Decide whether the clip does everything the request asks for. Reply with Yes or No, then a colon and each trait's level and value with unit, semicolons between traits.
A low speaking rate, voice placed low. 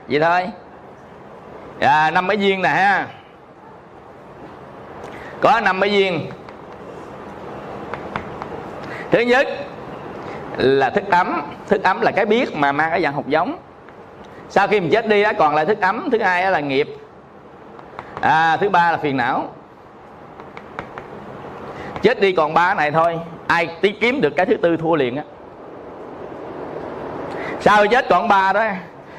No: slow, 145 wpm; high, 190 Hz